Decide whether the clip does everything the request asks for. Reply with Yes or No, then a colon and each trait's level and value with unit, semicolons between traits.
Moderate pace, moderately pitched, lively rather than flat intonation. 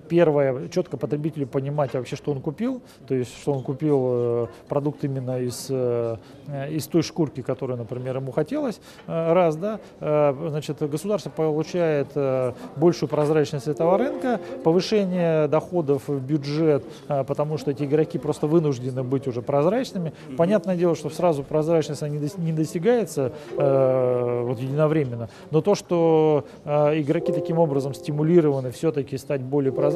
No: average, 130 wpm; medium, 150 Hz; average, 3.2 semitones